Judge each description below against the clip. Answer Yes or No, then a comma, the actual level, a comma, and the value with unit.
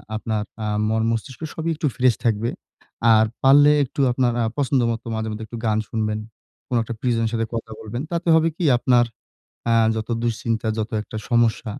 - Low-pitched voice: Yes, low, 115 Hz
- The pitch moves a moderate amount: No, narrow, 2.2 semitones